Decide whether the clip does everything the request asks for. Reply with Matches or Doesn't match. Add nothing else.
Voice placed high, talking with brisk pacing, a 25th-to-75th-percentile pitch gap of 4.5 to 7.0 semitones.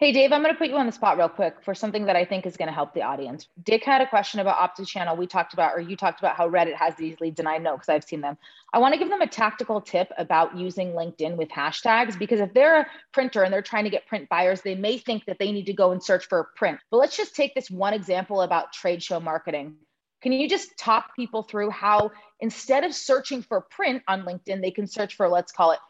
Matches